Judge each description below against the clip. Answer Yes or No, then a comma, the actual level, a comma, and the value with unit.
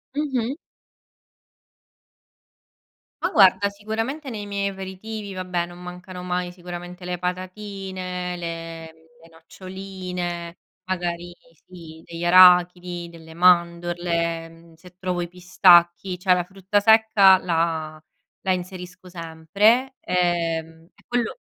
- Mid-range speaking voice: Yes, medium, 180 Hz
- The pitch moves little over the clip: Yes, narrow, 1.9 semitones